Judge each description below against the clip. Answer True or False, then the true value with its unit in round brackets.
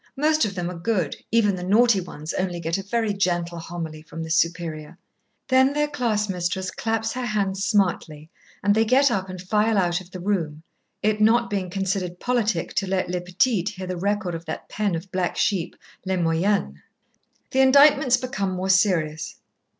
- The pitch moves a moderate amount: True (3.8 semitones)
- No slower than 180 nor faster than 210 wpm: True (185 wpm)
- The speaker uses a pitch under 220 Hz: True (190 Hz)